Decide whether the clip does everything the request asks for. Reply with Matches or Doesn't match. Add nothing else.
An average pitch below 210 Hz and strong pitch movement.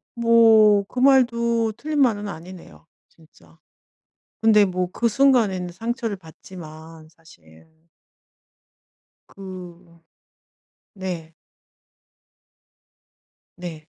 Matches